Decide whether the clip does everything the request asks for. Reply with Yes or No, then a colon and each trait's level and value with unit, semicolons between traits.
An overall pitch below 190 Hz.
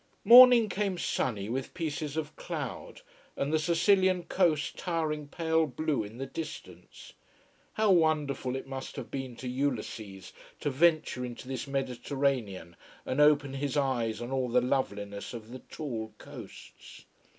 Yes: medium, 140 Hz